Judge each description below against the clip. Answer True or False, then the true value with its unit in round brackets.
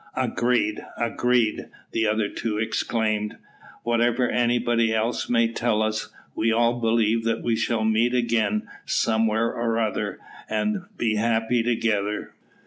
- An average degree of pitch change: False (1.4 semitones)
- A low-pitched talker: True (115 Hz)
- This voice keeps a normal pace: False (130 wpm)